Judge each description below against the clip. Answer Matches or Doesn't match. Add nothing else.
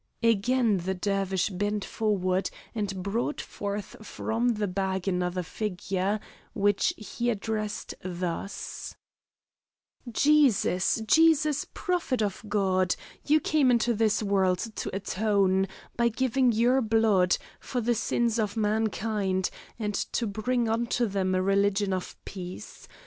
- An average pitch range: Matches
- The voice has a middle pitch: Doesn't match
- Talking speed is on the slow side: Matches